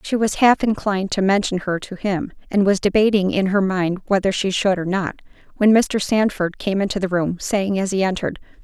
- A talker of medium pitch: No, high, 195 Hz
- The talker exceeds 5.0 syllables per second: Yes, 5.4 syllables/s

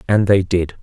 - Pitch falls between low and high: No, very low, 95 Hz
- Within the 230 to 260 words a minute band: No, fast, 215 wpm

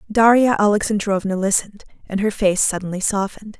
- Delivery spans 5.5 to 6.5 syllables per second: Yes, 6.0 syllables/s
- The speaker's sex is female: Yes, female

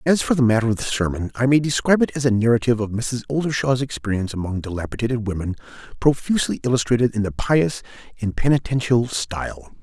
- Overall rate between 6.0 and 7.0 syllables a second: Yes, 6.5 syllables/s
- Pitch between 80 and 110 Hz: No, low, 120 Hz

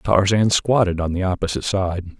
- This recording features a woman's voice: No, male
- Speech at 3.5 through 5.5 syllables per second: Yes, 5.3 syllables/s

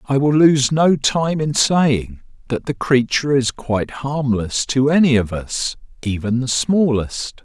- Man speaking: Yes, male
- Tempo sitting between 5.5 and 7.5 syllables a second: No, 4.0 syllables/s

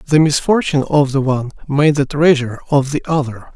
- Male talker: Yes, male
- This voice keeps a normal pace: Yes, average, 185 wpm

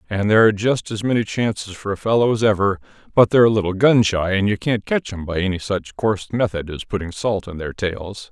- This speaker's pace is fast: Yes, fast, 240 wpm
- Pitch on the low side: Yes, low, 100 Hz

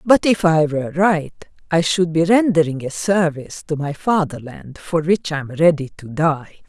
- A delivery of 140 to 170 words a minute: No, average, 190 wpm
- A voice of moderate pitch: Yes, medium, 160 Hz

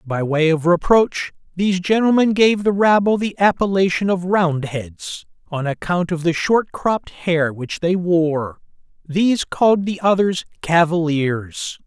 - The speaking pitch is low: No, medium, 180 Hz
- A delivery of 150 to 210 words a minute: No, average, 140 wpm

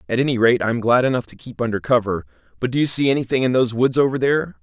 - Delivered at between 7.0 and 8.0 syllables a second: Yes, 7.1 syllables/s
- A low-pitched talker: Yes, low, 120 Hz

